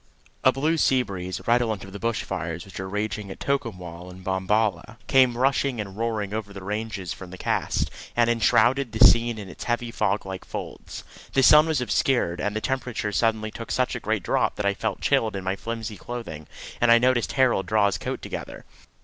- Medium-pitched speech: No, low, 110 Hz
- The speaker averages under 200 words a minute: No, fast, 205 wpm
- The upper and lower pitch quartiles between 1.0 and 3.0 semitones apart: No, average, 3.7 semitones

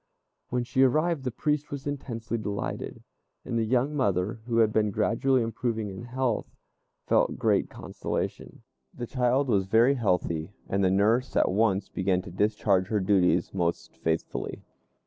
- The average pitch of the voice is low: Yes, low, 110 Hz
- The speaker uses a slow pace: No, average, 155 wpm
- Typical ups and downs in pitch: Yes, average, 4.6 semitones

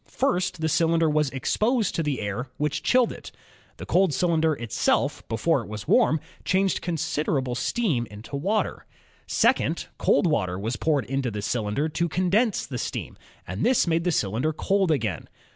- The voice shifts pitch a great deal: Yes, wide, 6.6 semitones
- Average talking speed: Yes, average, 170 wpm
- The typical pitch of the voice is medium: Yes, medium, 150 Hz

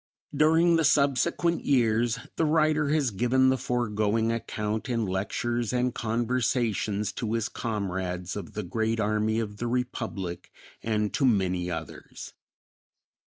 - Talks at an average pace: No, slow, 130 wpm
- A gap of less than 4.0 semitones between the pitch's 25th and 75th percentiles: Yes, average, 3.4 semitones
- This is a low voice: Yes, low, 115 Hz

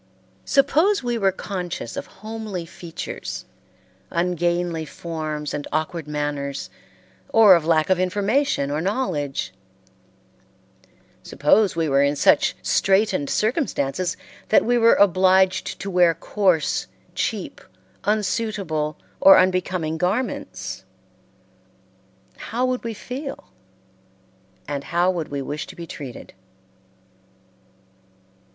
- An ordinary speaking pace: No, slow, 105 wpm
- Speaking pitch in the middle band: Yes, medium, 180 Hz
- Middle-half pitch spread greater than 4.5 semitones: Yes, average, 5.2 semitones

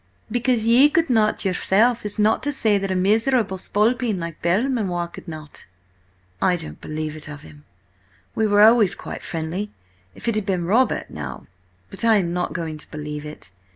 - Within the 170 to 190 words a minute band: Yes, average, 180 wpm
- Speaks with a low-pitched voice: No, high, 195 Hz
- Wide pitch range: Yes, wide, 5.7 semitones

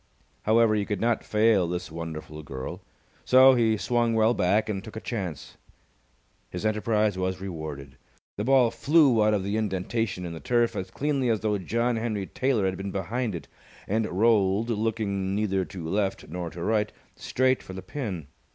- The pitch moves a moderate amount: Yes, average, 3.6 semitones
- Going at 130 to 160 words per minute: No, average, 180 wpm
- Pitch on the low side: Yes, low, 105 Hz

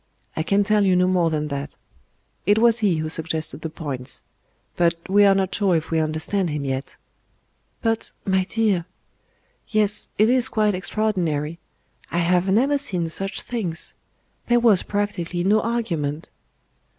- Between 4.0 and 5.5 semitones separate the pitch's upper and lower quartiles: Yes, average, 4.7 semitones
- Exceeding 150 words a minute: Yes, average, 160 wpm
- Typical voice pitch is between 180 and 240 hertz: Yes, medium, 185 Hz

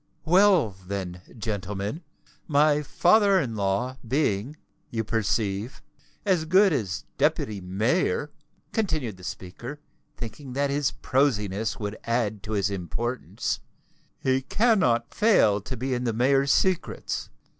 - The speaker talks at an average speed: No, slow, 125 wpm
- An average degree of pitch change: No, wide, 6.4 semitones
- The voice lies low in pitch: Yes, low, 125 Hz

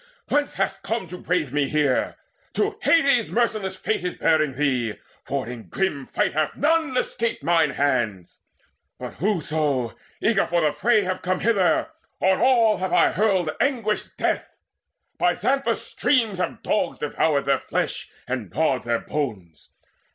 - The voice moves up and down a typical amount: No, wide, 7.6 semitones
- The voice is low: No, medium, 180 Hz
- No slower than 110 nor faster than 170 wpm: Yes, average, 150 wpm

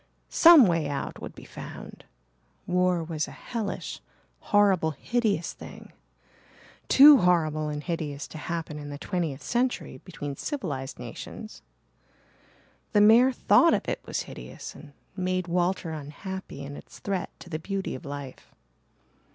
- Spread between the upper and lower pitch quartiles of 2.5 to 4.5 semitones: No, average, 5.1 semitones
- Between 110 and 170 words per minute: Yes, average, 140 wpm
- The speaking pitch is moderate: Yes, medium, 170 Hz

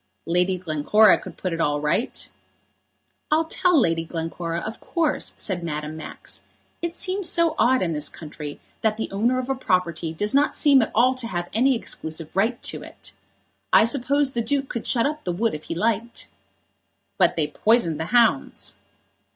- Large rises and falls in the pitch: Yes, wide, 7.8 semitones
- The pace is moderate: Yes, average, 180 wpm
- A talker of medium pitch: No, high, 220 Hz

